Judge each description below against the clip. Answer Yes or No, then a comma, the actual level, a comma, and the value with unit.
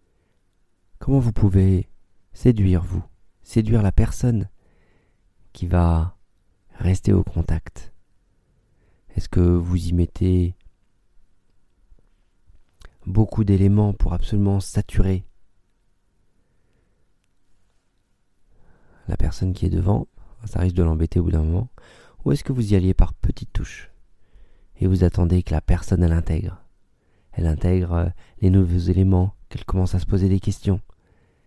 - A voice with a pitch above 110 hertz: No, very low, 95 Hz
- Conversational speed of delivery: No, slow, 125 wpm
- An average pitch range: No, narrow, 1.8 semitones